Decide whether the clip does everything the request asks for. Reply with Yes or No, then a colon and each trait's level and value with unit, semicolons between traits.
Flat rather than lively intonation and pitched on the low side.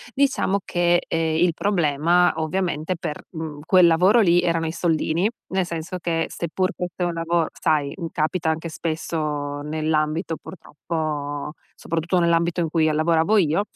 No: narrow, 2.0 semitones; medium, 165 Hz